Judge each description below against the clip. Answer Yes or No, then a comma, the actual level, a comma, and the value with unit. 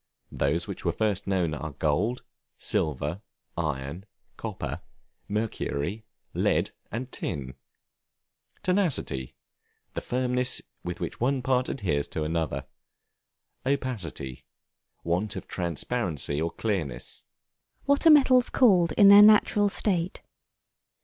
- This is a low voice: Yes, low, 100 Hz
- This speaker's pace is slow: Yes, slow, 110 wpm